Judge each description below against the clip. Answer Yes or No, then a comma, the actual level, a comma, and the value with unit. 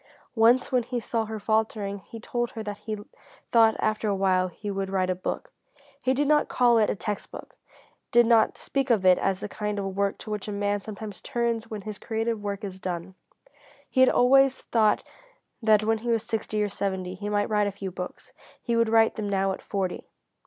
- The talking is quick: Yes, fast, 215 wpm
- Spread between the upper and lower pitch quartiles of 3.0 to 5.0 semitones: No, narrow, 2.5 semitones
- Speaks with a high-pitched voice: Yes, high, 215 Hz